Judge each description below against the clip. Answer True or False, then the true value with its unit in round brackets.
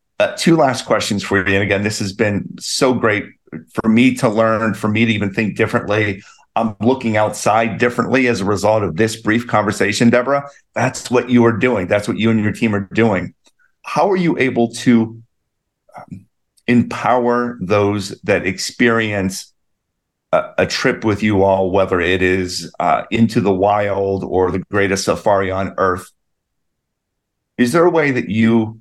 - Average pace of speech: True (170 wpm)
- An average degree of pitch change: True (3.3 semitones)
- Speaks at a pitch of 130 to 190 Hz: False (110 Hz)